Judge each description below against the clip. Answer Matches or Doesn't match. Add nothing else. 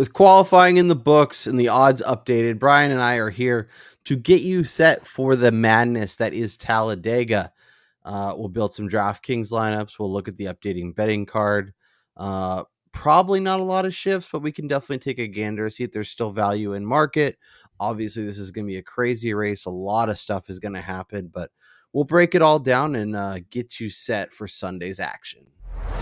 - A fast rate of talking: Matches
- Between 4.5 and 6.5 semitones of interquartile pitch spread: Matches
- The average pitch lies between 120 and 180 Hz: Doesn't match